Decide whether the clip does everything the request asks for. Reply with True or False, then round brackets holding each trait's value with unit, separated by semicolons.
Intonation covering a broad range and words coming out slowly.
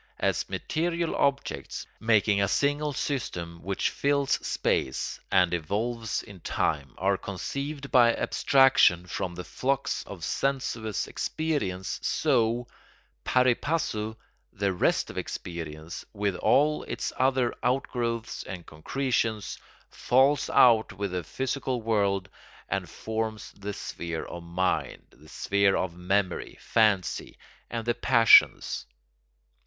True (5.9 semitones; 115 wpm)